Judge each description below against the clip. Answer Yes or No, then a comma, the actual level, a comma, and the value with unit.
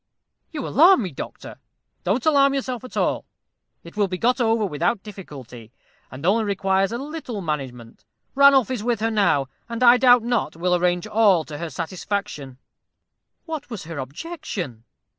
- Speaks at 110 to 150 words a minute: No, average, 160 wpm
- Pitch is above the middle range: Yes, high, 205 Hz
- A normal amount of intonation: No, wide, 7.0 semitones